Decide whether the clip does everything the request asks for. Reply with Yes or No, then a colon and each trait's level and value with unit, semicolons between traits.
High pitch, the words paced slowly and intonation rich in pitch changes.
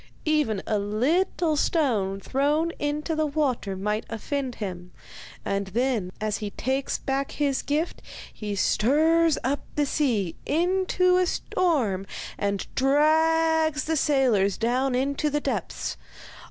Yes: very high, 275 Hz; slow, 125 wpm; wide, 6.5 semitones